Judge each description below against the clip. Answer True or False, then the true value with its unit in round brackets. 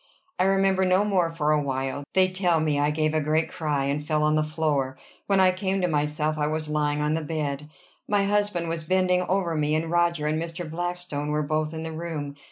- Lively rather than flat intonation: False (2.9 semitones)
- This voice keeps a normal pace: False (225 wpm)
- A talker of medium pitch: True (155 Hz)